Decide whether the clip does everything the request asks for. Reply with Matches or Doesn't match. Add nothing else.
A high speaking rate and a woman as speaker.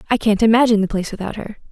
Matches